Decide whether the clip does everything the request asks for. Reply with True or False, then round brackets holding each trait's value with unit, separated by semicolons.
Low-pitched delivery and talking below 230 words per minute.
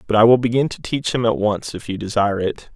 False (110 Hz; 285 wpm)